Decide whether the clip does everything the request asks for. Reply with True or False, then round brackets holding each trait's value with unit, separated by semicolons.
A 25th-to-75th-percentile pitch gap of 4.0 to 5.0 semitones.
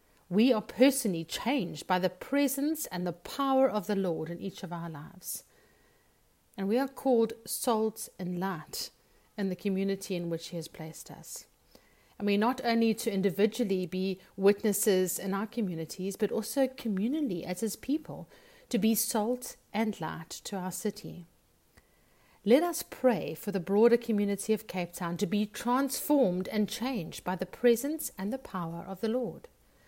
True (4.4 semitones)